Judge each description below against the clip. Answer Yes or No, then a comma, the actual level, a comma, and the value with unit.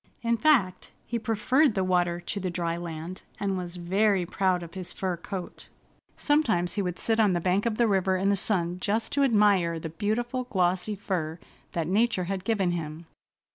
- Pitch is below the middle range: No, high, 190 Hz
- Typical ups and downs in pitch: Yes, average, 3.6 semitones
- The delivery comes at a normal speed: Yes, average, 190 wpm